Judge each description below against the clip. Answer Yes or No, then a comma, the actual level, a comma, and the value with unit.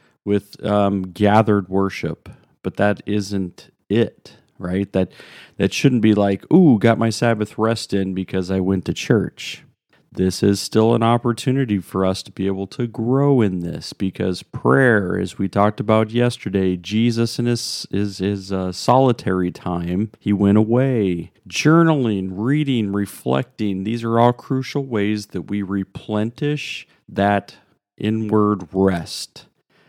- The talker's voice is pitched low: Yes, low, 105 Hz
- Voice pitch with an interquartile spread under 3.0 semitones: No, average, 3.3 semitones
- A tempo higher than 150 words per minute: No, average, 145 wpm